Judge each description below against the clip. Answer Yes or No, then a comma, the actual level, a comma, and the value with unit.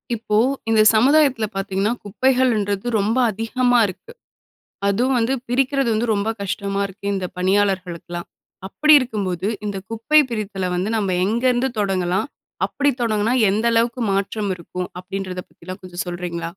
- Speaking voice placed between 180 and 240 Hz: Yes, high, 205 Hz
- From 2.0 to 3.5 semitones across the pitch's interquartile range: No, average, 4.0 semitones